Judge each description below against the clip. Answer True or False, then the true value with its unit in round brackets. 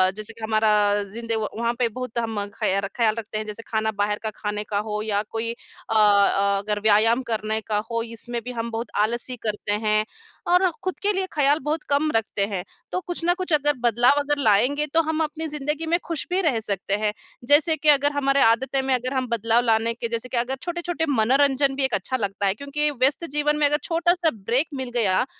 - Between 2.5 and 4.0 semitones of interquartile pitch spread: False (5.1 semitones)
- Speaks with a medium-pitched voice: False (235 Hz)